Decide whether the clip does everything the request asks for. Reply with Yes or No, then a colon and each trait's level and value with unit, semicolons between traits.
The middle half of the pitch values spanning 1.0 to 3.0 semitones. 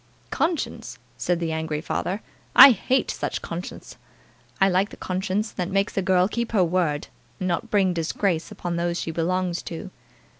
Yes: narrow, 2.5 semitones